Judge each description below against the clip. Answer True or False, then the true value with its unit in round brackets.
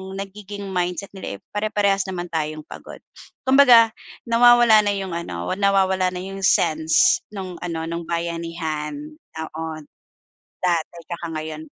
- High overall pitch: False (180 Hz)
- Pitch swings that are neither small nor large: True (3.7 semitones)